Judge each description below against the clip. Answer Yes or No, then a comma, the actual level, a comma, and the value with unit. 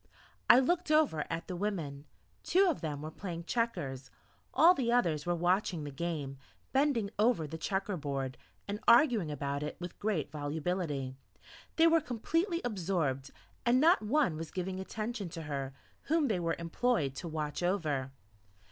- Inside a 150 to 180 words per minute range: Yes, average, 160 wpm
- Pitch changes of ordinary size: No, wide, 7.8 semitones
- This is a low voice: No, medium, 175 Hz